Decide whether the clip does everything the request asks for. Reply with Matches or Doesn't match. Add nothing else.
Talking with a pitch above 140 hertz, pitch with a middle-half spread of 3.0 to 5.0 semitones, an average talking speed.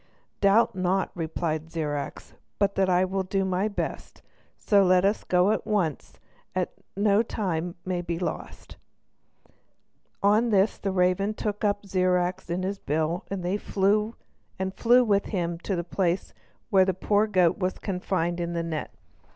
Doesn't match